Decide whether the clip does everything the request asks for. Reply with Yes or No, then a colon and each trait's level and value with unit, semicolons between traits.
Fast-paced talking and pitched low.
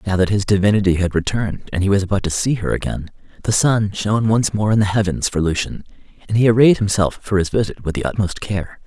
Yes: fast, 235 wpm; low, 100 Hz